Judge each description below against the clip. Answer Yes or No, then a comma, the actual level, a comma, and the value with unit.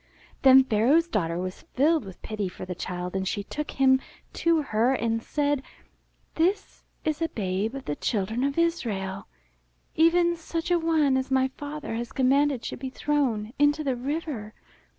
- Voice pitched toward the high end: Yes, very high, 265 Hz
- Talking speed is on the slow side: No, average, 170 wpm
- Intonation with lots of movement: Yes, wide, 6.0 semitones